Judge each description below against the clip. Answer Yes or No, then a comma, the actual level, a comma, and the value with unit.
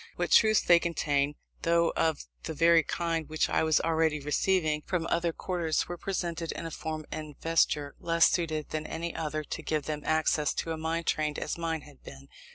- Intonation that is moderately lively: No, narrow, 1.6 semitones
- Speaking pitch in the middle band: Yes, medium, 160 Hz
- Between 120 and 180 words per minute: No, average, 195 wpm